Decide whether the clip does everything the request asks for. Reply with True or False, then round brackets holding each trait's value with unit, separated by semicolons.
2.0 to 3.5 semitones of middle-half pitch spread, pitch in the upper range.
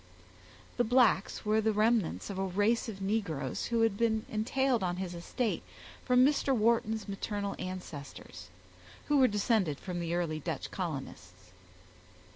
False (4.4 semitones; 205 Hz)